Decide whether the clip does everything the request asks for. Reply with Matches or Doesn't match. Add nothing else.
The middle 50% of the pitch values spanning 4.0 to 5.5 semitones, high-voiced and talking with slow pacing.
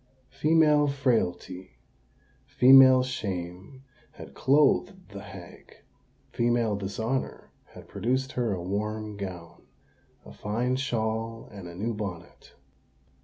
Doesn't match